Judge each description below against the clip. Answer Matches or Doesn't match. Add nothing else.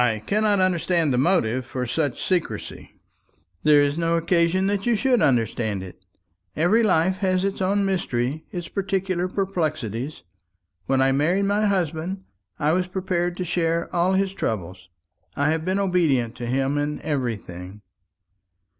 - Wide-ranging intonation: Matches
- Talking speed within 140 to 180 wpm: Matches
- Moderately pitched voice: Matches